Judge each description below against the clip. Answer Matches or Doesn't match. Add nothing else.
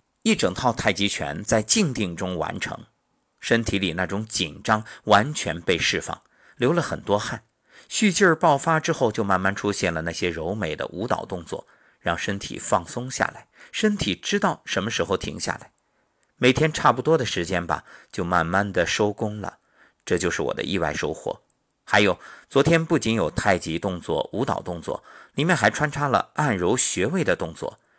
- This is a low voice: Matches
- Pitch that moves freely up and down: Matches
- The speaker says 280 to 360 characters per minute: Doesn't match